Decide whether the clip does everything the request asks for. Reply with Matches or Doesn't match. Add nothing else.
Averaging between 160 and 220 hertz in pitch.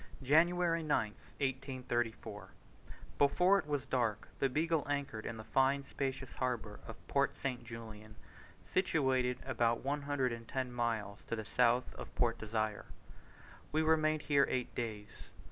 Doesn't match